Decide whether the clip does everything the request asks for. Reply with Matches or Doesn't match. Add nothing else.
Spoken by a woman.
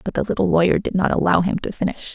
Matches